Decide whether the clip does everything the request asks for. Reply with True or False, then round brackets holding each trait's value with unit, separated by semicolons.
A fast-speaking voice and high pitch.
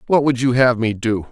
False (275 wpm; 125 Hz)